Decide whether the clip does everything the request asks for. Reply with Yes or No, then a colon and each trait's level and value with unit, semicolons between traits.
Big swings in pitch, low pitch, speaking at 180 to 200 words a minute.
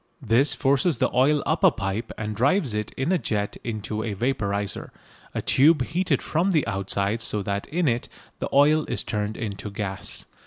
Yes: wide, 6.1 semitones; low, 115 Hz; average, 185 wpm